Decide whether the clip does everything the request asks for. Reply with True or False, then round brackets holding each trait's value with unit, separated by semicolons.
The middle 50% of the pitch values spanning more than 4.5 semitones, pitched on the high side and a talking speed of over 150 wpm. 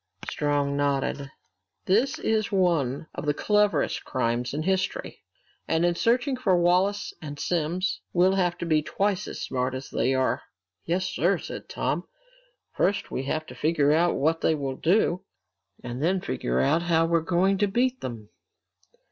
False (5.0 semitones; 170 Hz; 165 wpm)